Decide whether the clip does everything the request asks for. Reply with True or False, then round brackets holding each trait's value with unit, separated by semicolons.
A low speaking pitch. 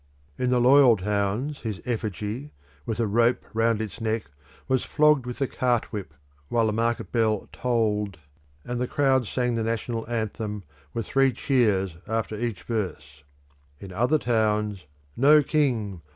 True (115 Hz)